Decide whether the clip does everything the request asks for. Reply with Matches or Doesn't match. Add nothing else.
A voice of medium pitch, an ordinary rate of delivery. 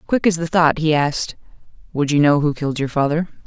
Doesn't match